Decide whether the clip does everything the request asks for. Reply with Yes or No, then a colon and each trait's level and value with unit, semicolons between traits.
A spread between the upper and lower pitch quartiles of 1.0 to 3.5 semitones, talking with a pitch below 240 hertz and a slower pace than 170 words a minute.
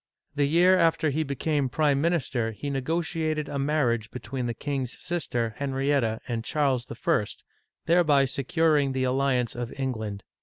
No: average, 3.9 semitones; medium, 140 Hz; average, 150 wpm